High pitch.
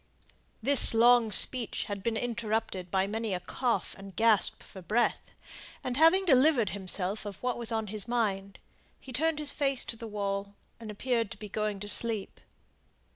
Yes: high, 225 Hz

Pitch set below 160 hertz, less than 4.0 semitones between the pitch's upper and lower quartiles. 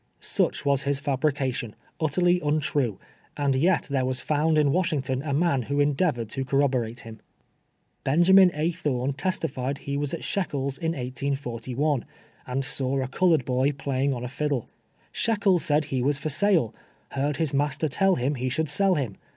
Yes: medium, 140 Hz; average, 2.9 semitones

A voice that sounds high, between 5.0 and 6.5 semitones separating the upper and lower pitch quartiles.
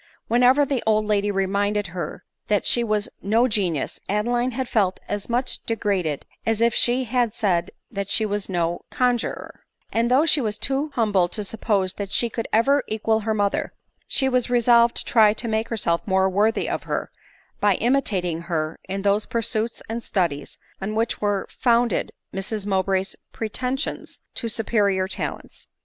No: high, 215 Hz; average, 3.3 semitones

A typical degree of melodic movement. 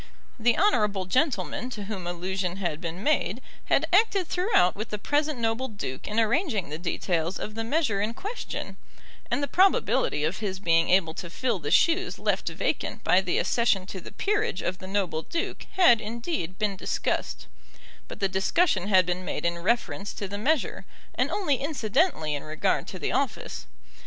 No: wide, 7.4 semitones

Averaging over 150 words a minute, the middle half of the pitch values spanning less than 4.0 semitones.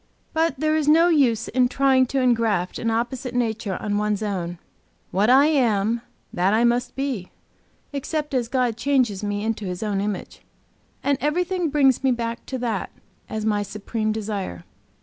No: average, 170 wpm; average, 4.4 semitones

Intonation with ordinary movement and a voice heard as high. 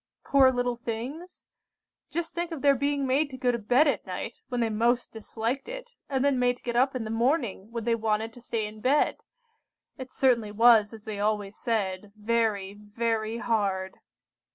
Yes: average, 3.3 semitones; high, 235 Hz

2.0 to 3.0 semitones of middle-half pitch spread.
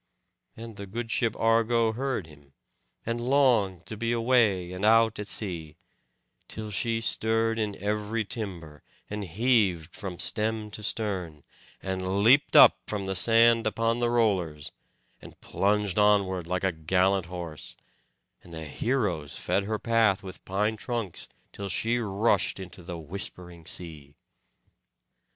No: average, 3.9 semitones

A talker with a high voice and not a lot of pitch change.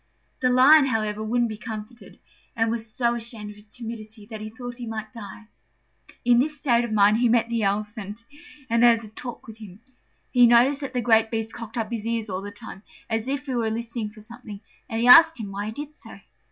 Yes: high, 230 Hz; narrow, 2.0 semitones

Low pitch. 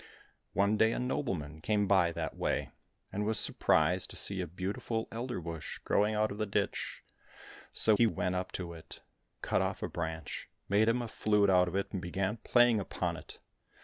Yes: low, 100 Hz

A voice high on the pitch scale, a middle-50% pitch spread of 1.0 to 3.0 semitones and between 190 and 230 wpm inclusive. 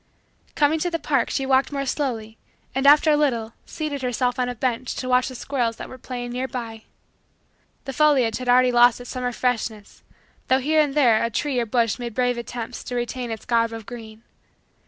Yes: very high, 250 Hz; narrow, 2.5 semitones; average, 200 wpm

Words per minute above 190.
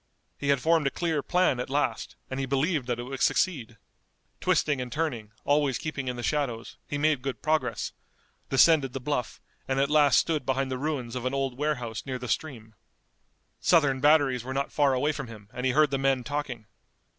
Yes: average, 200 wpm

